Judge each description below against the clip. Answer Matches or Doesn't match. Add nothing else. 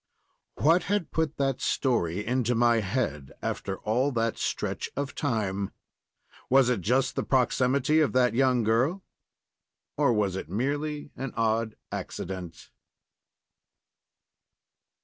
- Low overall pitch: Matches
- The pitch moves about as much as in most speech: Matches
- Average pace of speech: Doesn't match